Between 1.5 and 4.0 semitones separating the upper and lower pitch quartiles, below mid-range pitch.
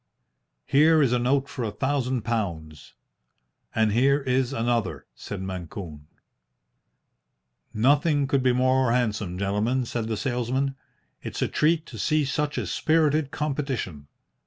No: average, 4.5 semitones; low, 125 Hz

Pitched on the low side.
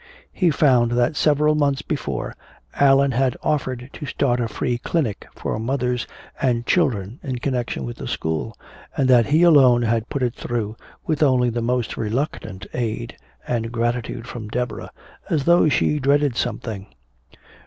Yes: low, 125 Hz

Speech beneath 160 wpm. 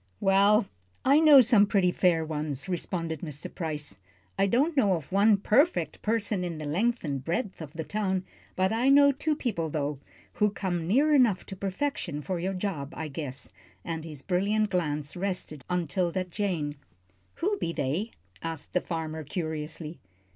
No: average, 170 wpm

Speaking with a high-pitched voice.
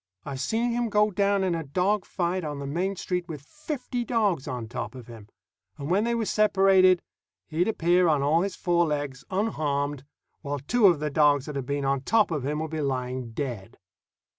No: medium, 160 Hz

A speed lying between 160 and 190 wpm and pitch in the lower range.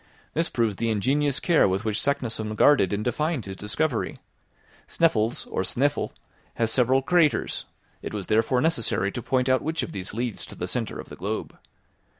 Yes: average, 175 wpm; low, 120 Hz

